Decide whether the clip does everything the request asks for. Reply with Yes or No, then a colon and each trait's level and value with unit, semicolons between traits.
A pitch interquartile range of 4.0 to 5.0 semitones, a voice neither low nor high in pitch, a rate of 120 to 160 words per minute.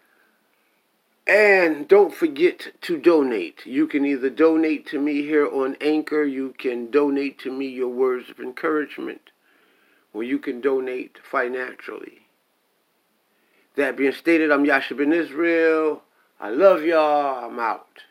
Yes: average, 4.3 semitones; medium, 150 Hz; slow, 135 wpm